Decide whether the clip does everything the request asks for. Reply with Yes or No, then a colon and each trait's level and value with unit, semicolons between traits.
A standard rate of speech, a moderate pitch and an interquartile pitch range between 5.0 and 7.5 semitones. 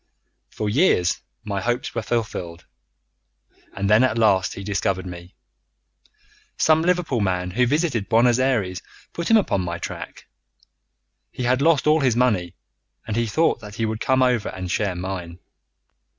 No: average, 155 wpm; low, 110 Hz; average, 5.3 semitones